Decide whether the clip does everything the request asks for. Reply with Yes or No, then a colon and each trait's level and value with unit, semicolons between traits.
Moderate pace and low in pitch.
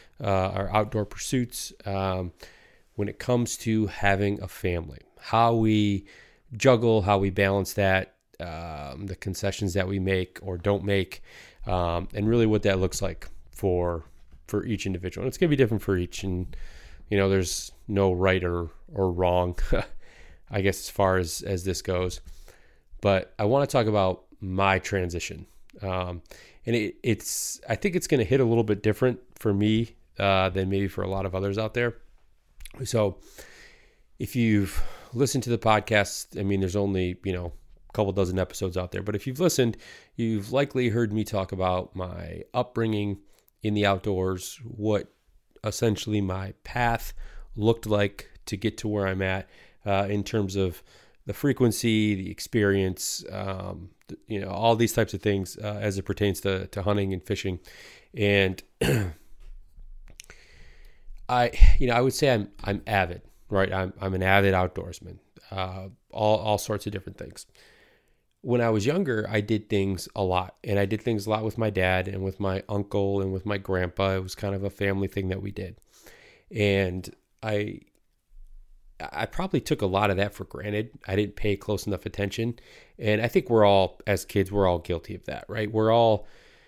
Yes: average, 180 wpm; low, 100 Hz